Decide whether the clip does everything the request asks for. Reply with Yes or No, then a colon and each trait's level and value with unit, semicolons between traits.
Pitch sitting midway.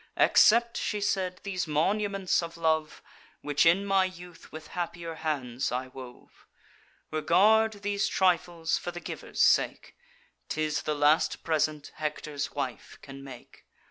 Yes: medium, 165 Hz